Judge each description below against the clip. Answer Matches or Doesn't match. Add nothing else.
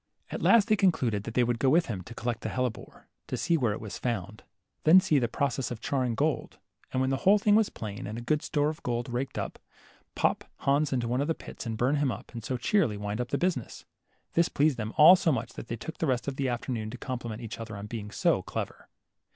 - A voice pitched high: Doesn't match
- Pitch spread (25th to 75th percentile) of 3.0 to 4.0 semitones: Doesn't match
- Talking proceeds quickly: Matches